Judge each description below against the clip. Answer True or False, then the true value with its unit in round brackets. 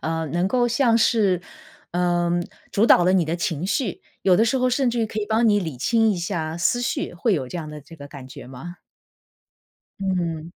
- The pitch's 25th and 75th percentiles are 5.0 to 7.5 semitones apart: True (5.3 semitones)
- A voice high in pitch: False (180 Hz)